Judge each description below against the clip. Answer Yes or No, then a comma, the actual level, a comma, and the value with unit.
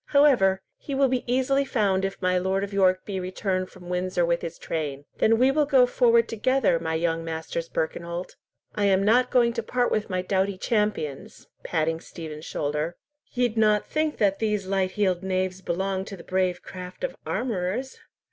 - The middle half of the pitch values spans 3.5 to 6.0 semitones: Yes, average, 4.5 semitones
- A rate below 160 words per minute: No, average, 180 wpm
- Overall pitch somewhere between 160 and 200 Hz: Yes, high, 190 Hz